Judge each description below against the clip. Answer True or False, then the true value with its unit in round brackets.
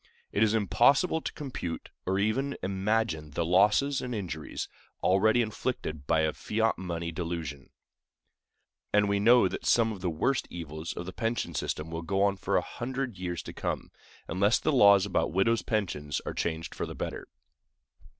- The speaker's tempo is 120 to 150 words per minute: False (170 wpm)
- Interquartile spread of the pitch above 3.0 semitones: True (5.1 semitones)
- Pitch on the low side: True (100 Hz)